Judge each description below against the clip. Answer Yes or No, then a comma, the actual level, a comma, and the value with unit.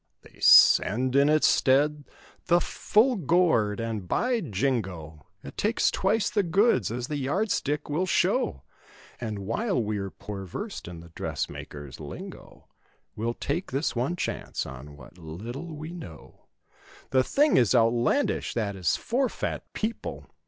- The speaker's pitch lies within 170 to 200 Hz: No, low, 130 Hz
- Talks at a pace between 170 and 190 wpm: No, average, 150 wpm